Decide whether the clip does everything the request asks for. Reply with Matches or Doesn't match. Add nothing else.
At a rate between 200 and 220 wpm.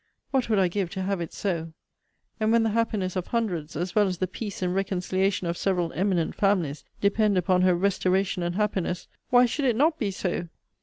Matches